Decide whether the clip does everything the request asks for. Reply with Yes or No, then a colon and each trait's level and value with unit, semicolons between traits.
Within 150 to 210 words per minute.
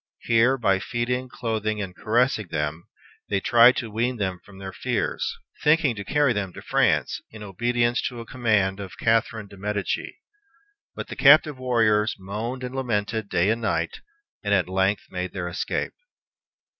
Yes: average, 165 wpm